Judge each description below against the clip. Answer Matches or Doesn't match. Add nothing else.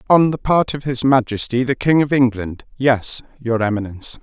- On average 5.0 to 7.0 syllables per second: Matches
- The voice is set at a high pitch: Doesn't match